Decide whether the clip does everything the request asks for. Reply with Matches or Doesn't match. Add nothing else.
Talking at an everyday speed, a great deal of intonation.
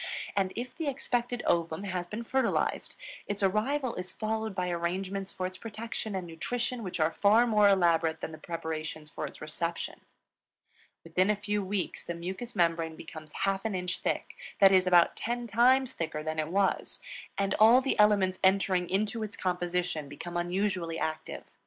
Doesn't match